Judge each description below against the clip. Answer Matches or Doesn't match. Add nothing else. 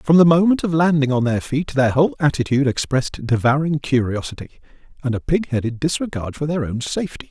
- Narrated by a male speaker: Matches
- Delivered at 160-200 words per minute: Matches